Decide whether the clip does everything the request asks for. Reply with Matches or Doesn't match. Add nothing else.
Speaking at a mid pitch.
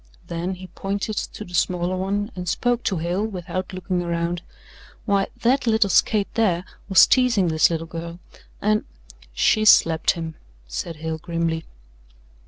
Matches